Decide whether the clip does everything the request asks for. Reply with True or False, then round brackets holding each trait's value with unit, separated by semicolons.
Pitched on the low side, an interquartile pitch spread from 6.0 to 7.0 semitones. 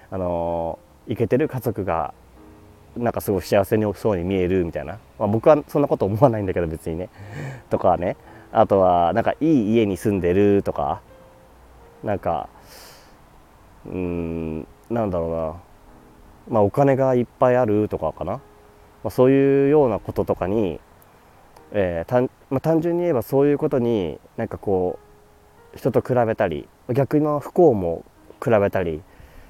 True (105 Hz; 6.5 semitones)